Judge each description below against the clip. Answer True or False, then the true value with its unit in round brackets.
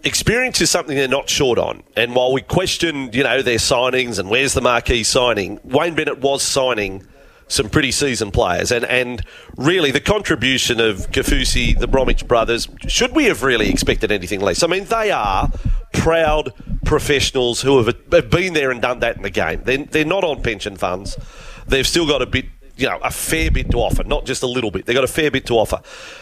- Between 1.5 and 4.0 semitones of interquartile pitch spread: False (4.4 semitones)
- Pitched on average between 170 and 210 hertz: False (135 Hz)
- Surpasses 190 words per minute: True (205 wpm)